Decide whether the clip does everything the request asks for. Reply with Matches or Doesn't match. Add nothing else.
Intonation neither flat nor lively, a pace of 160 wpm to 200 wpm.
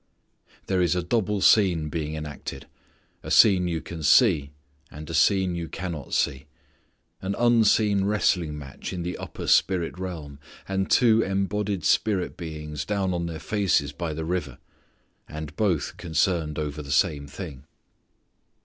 Doesn't match